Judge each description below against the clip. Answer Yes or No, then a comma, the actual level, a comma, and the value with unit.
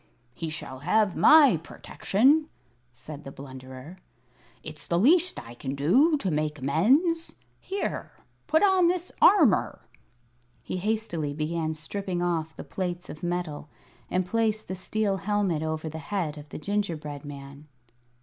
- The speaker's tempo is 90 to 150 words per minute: Yes, average, 140 wpm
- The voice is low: No, medium, 175 Hz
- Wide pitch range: Yes, wide, 6.2 semitones